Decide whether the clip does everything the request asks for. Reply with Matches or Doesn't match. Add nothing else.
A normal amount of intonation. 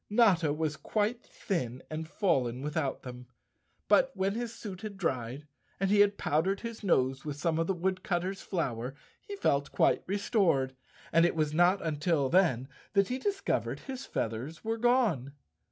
Doesn't match